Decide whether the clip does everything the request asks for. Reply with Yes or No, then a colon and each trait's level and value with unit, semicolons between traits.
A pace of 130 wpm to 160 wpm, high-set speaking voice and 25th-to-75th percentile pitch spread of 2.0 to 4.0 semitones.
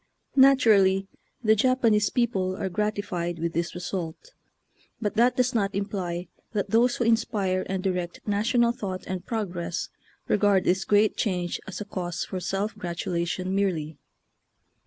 Yes: average, 145 wpm; high, 195 Hz; average, 3.3 semitones